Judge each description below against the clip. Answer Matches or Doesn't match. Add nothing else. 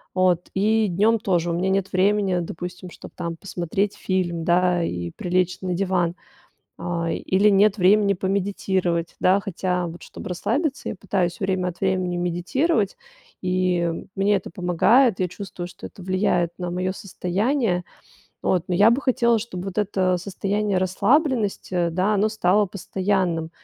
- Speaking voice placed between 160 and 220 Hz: Matches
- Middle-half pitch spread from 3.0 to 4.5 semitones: Doesn't match